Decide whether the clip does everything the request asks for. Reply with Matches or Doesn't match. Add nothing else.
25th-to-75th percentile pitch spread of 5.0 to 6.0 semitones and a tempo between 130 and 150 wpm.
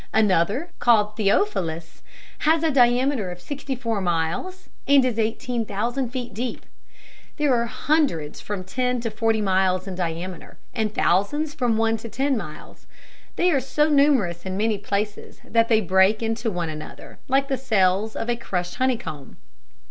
Doesn't match